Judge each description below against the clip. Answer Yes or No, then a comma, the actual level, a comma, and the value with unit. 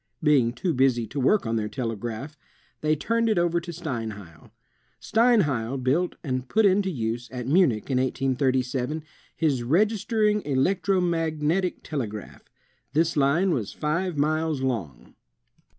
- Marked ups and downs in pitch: Yes, wide, 5.8 semitones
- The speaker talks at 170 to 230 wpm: No, slow, 135 wpm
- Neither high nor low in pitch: Yes, medium, 145 Hz